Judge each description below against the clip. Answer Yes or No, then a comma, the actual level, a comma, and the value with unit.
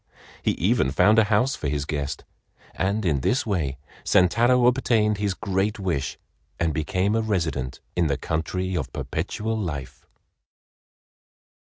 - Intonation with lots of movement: Yes, wide, 6.1 semitones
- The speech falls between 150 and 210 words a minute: No, average, 140 wpm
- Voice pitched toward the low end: Yes, very low, 95 Hz